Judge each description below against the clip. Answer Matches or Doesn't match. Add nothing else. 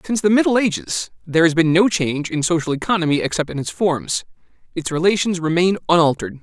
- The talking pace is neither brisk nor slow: Matches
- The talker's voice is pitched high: Doesn't match